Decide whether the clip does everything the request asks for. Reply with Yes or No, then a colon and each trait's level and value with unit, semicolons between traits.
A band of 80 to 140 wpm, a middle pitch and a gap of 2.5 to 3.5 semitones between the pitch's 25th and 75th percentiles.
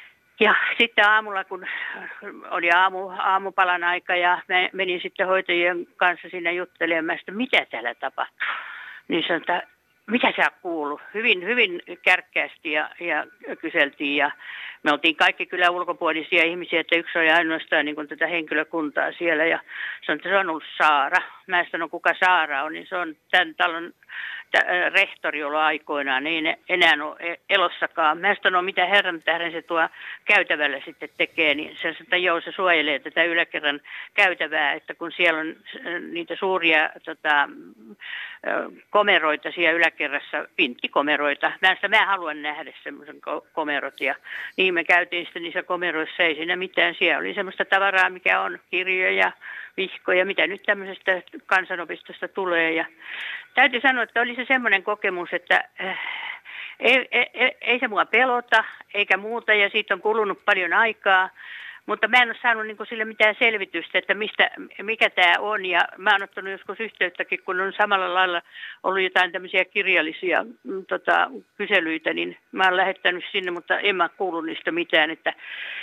No: average, 150 wpm; medium, 180 Hz; average, 3.2 semitones